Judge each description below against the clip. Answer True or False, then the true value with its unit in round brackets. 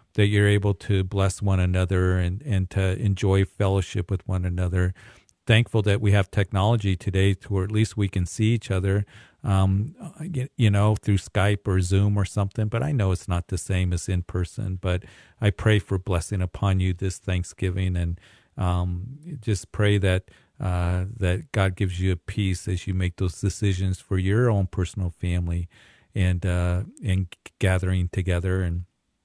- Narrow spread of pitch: True (2.0 semitones)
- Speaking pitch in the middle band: False (95 Hz)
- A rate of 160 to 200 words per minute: True (175 wpm)